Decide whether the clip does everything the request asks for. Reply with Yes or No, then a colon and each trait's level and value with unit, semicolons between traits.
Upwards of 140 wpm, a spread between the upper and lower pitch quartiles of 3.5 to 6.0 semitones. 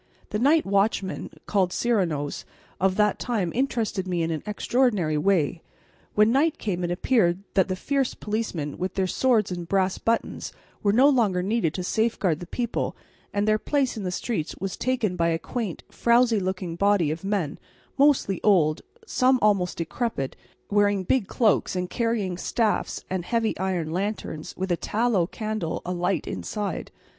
Yes: average, 165 wpm; average, 4.4 semitones